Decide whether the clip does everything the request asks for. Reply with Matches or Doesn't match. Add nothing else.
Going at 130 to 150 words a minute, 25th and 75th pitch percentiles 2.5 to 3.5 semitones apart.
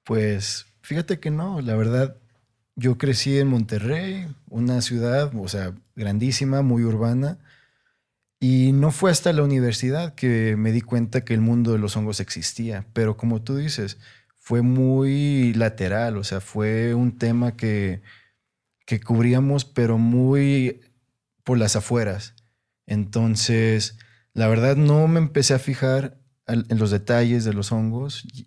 Matches